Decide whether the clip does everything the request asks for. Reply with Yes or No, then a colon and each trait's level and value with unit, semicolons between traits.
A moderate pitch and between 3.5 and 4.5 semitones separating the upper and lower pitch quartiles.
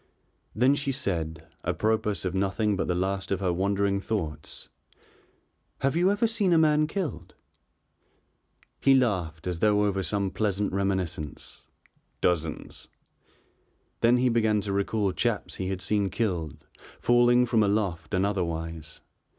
No: low, 100 Hz; average, 4.2 semitones